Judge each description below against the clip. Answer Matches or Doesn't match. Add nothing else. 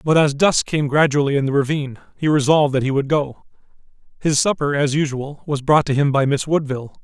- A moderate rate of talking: Doesn't match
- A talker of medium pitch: Matches